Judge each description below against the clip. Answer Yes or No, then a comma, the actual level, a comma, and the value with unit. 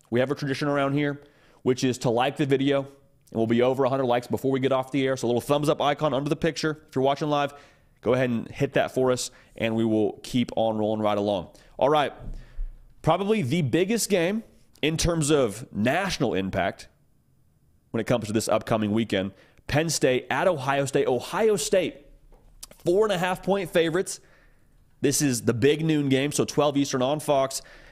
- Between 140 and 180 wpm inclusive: No, average, 200 wpm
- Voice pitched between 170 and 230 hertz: No, medium, 140 Hz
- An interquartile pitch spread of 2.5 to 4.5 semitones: Yes, average, 4.0 semitones